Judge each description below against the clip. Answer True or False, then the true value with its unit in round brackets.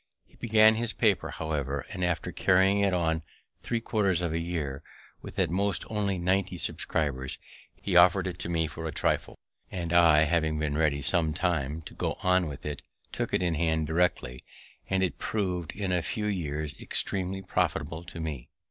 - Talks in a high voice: False (85 Hz)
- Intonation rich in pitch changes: False (3.4 semitones)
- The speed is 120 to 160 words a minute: False (185 wpm)